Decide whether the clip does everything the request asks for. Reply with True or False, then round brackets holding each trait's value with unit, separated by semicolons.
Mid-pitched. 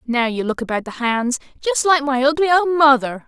False (275 Hz)